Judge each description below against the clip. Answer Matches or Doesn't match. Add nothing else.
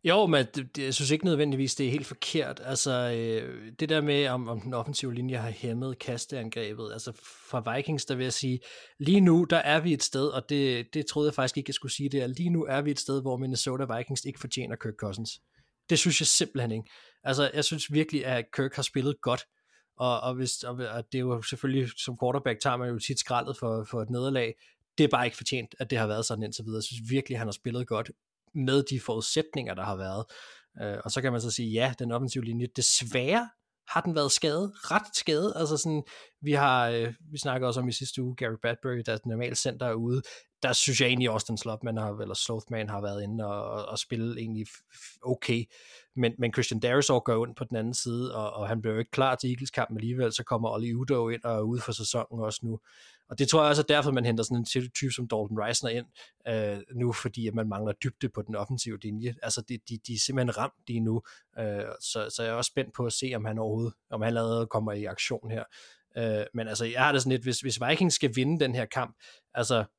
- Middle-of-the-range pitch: Doesn't match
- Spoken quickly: Matches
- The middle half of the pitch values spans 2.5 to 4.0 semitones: Matches